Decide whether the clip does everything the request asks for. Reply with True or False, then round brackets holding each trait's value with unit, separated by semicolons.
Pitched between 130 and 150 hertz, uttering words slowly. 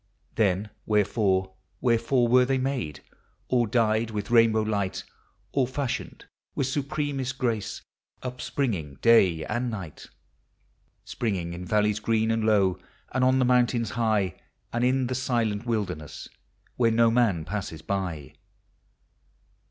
False (115 Hz; 130 wpm)